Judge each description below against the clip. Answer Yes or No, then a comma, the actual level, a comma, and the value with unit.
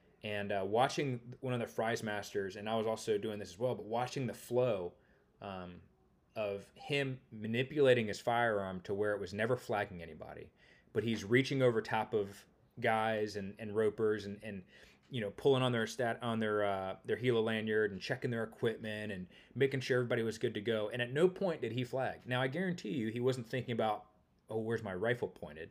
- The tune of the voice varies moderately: Yes, average, 3.1 semitones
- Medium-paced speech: No, fast, 210 wpm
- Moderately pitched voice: No, low, 115 Hz